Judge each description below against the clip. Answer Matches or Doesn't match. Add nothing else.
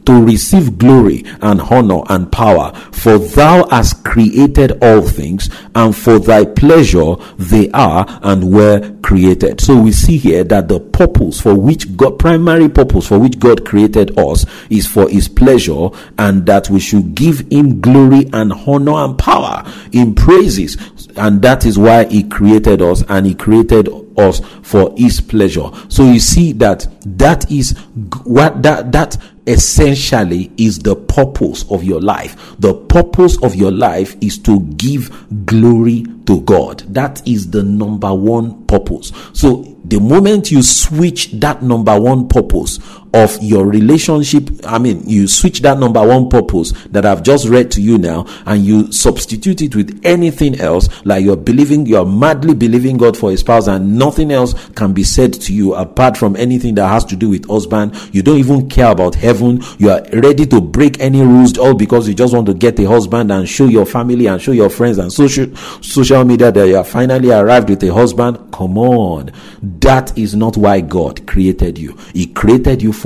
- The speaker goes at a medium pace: Matches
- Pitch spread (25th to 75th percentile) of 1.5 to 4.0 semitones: Doesn't match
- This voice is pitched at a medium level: Doesn't match